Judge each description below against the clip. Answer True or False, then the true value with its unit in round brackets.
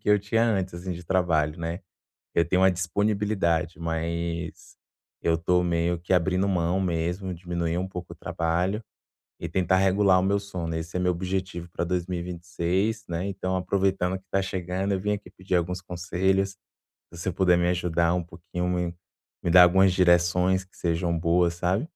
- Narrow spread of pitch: True (1.8 semitones)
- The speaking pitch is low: True (90 Hz)